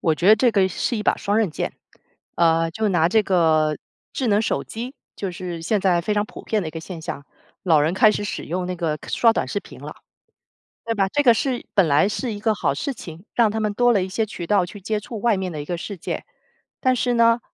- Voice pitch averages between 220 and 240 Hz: No, high, 200 Hz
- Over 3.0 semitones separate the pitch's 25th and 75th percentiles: Yes, average, 4.4 semitones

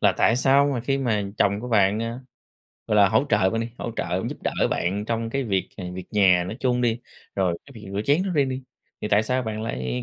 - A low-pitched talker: Yes, low, 110 Hz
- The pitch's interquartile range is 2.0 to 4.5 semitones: Yes, average, 3.8 semitones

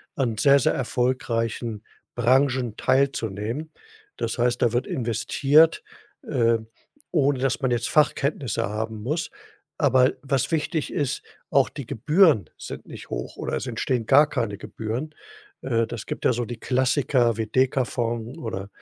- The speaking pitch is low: Yes, low, 125 Hz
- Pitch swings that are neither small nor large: Yes, average, 3.4 semitones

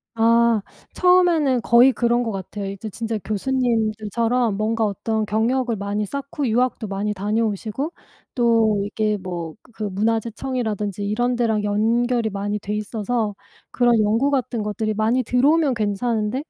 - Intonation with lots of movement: No, average, 2.7 semitones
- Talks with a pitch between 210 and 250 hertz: Yes, high, 225 Hz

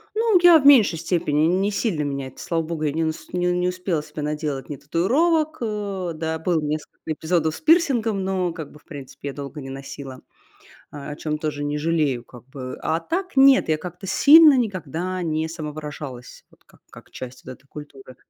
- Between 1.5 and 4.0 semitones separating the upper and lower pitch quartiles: No, average, 4.6 semitones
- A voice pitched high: No, medium, 160 Hz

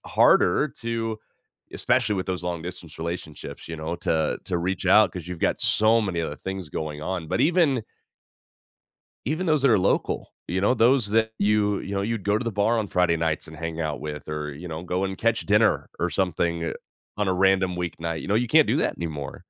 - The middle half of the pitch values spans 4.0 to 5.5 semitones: Yes, average, 4.4 semitones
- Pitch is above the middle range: No, very low, 95 Hz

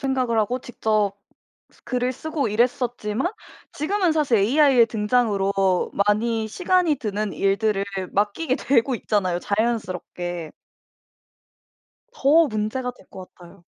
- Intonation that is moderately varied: Yes, average, 4.4 semitones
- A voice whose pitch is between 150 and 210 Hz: No, high, 225 Hz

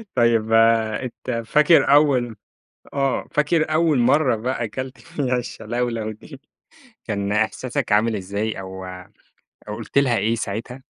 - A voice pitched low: Yes, low, 120 Hz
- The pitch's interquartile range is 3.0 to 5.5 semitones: Yes, average, 3.7 semitones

